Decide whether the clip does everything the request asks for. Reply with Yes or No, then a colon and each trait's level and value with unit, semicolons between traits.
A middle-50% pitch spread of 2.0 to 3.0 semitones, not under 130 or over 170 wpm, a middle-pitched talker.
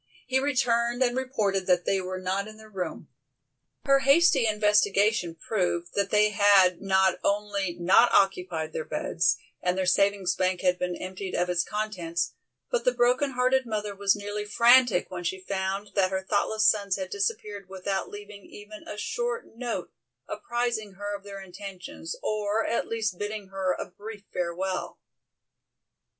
No: narrow, 2.6 semitones; average, 160 wpm; high, 200 Hz